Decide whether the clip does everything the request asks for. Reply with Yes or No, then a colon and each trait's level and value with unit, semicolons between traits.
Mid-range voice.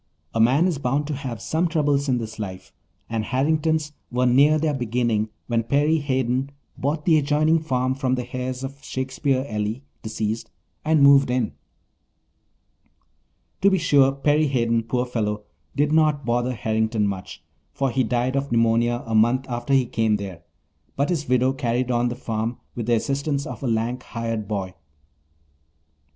No: low, 125 Hz